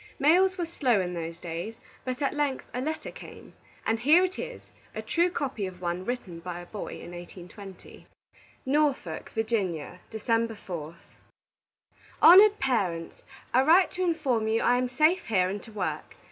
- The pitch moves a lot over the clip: Yes, wide, 8.6 semitones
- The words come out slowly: No, average, 165 wpm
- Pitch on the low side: No, high, 230 Hz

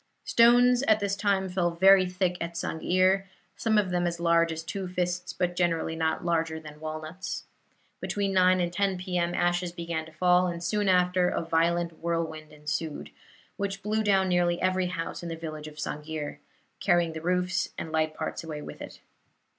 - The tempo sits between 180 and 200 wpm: Yes, average, 185 wpm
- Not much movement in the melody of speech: Yes, narrow, 2.3 semitones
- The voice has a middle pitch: Yes, medium, 175 Hz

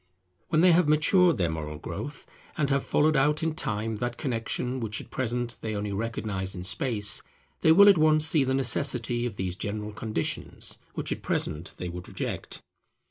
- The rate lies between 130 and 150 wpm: No, average, 185 wpm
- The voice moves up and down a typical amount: No, wide, 6.5 semitones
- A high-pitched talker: No, low, 120 Hz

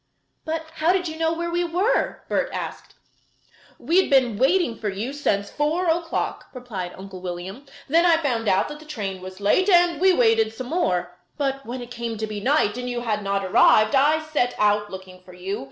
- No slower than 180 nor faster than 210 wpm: Yes, fast, 205 wpm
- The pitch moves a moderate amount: No, wide, 7.8 semitones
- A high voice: Yes, high, 245 Hz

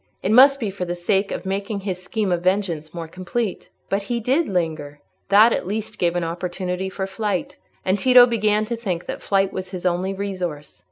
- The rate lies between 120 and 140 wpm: No, fast, 205 wpm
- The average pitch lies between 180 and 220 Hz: Yes, high, 190 Hz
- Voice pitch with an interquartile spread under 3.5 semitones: Yes, average, 3.1 semitones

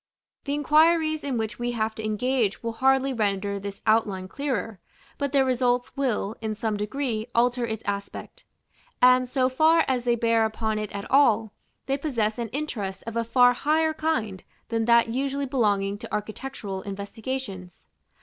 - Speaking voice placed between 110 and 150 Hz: No, high, 235 Hz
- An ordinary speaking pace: Yes, average, 165 wpm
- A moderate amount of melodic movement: Yes, average, 4.0 semitones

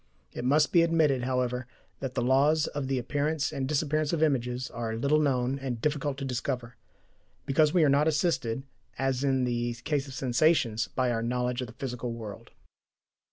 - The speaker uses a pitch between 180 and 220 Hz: No, low, 135 Hz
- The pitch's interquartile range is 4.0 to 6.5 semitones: No, average, 3.1 semitones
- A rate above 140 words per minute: Yes, average, 180 wpm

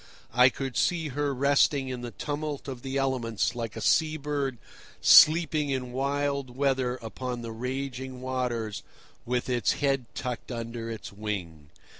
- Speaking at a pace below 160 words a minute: Yes, average, 150 wpm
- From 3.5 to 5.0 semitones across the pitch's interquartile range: No, average, 2.7 semitones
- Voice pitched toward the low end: Yes, low, 130 Hz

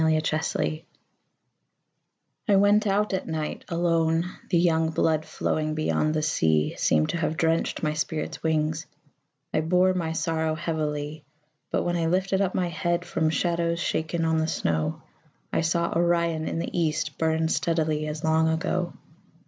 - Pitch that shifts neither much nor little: No, narrow, 1.6 semitones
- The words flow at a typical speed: Yes, average, 155 wpm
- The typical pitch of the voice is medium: Yes, medium, 160 Hz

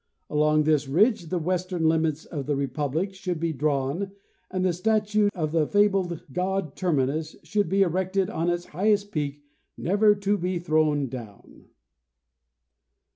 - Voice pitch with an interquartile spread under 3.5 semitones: No, average, 4.2 semitones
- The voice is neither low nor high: Yes, medium, 170 Hz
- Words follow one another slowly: No, average, 150 wpm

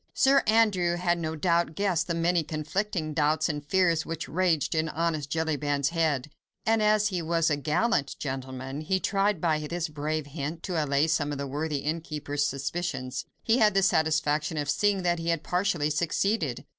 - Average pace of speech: Yes, average, 180 wpm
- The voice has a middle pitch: Yes, medium, 160 Hz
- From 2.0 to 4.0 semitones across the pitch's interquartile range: Yes, average, 3.1 semitones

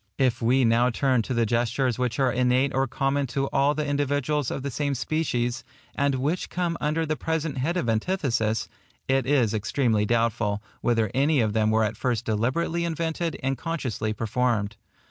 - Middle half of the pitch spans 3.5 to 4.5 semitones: Yes, average, 3.9 semitones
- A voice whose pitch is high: No, low, 130 Hz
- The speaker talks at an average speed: Yes, average, 180 wpm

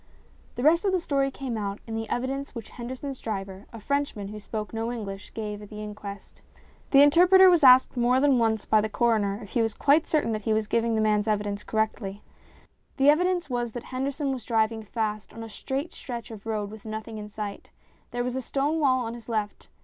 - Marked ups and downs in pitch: No, average, 4.1 semitones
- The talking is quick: Yes, fast, 220 wpm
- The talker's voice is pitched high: Yes, high, 230 Hz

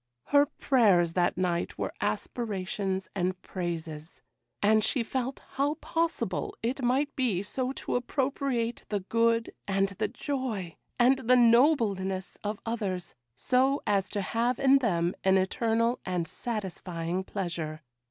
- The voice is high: Yes, high, 215 Hz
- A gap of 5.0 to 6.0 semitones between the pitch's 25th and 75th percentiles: Yes, wide, 5.4 semitones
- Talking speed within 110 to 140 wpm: Yes, slow, 135 wpm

